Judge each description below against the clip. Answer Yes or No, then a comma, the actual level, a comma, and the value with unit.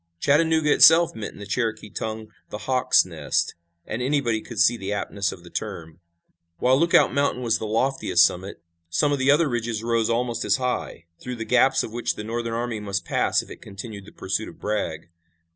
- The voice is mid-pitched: No, low, 115 Hz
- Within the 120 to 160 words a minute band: No, average, 200 wpm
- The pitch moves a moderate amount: Yes, average, 3.6 semitones